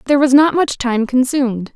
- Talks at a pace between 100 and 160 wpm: No, fast, 205 wpm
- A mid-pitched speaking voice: No, very high, 260 Hz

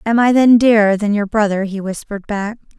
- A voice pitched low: No, high, 210 Hz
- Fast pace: Yes, fast, 215 wpm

